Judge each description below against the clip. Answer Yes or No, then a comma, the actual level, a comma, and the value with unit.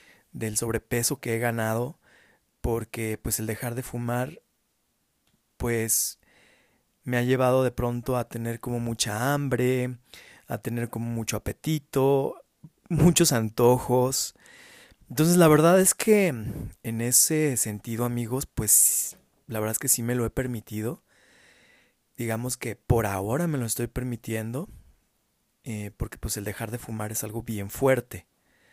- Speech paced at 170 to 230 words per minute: No, average, 140 wpm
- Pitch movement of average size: No, narrow, 2.3 semitones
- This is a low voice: Yes, low, 120 Hz